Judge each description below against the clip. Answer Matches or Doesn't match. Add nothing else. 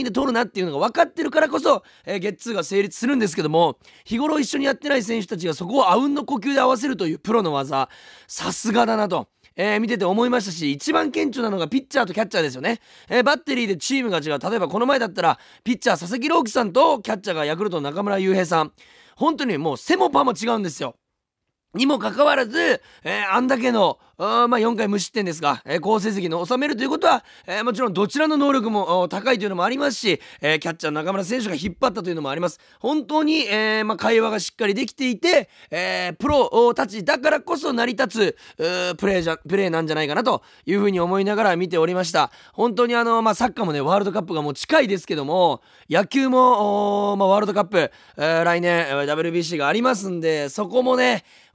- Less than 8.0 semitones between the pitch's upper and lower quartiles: Matches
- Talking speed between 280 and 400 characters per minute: Doesn't match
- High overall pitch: Matches